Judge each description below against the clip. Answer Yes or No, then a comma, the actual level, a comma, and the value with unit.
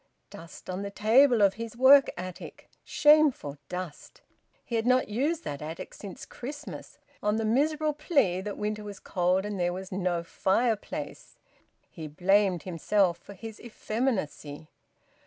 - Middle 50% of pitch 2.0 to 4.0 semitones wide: No, average, 5.2 semitones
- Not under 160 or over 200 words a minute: No, average, 145 wpm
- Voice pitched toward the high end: Yes, high, 205 Hz